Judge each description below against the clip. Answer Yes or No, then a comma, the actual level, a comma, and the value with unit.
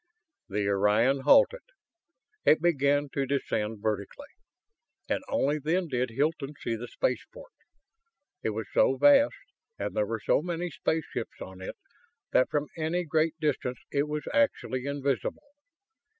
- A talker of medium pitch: Yes, medium, 145 Hz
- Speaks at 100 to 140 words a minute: Yes, slow, 135 wpm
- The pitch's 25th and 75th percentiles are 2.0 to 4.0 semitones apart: No, wide, 5.4 semitones